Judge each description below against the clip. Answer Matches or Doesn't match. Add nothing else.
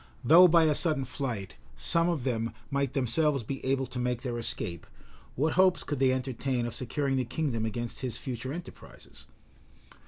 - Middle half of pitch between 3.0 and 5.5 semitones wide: Matches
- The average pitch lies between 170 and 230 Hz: Doesn't match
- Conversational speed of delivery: Matches